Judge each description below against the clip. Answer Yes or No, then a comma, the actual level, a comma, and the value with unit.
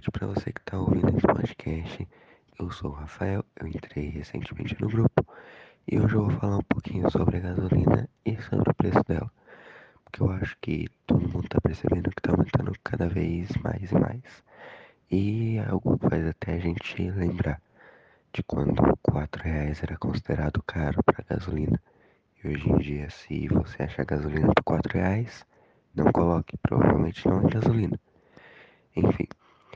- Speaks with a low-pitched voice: Yes, very low, 95 Hz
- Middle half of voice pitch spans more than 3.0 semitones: Yes, average, 5.1 semitones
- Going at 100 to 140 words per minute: No, average, 165 wpm